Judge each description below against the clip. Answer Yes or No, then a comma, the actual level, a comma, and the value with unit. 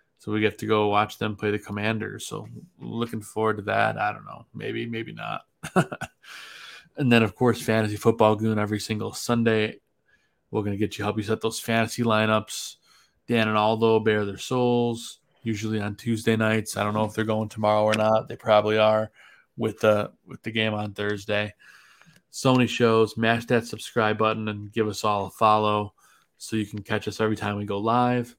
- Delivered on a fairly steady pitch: Yes, narrow, 1.3 semitones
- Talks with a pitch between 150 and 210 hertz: No, low, 110 Hz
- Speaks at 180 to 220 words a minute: Yes, average, 200 wpm